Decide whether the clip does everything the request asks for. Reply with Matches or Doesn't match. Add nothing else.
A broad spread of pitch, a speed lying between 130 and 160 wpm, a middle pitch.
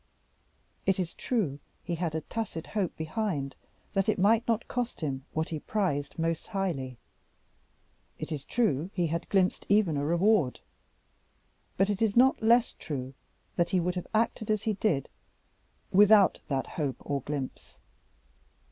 Matches